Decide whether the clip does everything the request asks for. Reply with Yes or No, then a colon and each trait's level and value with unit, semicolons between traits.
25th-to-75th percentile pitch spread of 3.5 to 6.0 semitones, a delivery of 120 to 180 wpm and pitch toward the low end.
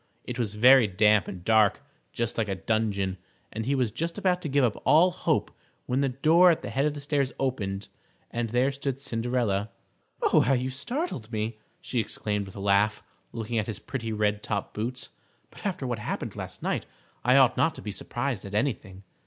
No: average, 4.4 semitones; average, 200 wpm; low, 115 Hz